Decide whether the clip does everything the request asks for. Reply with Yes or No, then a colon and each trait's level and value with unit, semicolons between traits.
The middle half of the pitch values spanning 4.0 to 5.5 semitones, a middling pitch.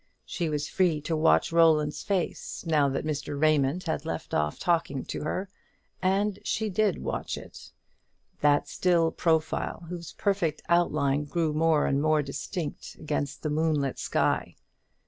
No: average, 2.8 semitones; medium, 155 Hz